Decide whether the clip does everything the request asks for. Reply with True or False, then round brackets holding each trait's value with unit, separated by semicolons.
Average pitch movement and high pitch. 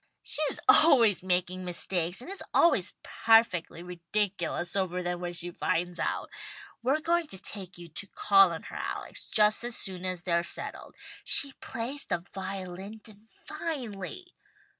True (4.6 semitones; 195 Hz)